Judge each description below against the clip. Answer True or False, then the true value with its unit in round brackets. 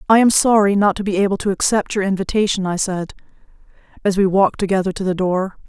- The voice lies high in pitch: True (195 Hz)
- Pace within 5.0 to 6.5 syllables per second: True (6.4 syllables/s)